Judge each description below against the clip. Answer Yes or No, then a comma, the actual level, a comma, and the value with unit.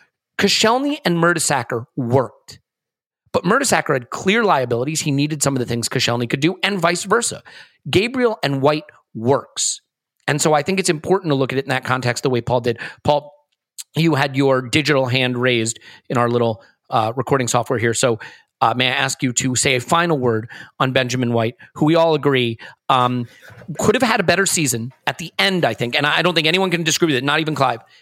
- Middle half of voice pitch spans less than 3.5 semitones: No, average, 4.8 semitones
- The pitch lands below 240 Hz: Yes, medium, 140 Hz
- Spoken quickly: Yes, fast, 210 wpm